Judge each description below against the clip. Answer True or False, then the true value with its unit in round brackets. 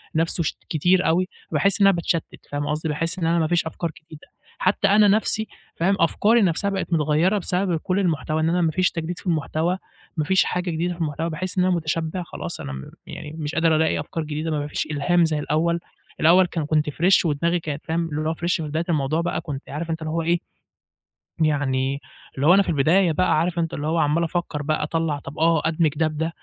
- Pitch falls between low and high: True (165 Hz)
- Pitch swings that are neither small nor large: False (2.3 semitones)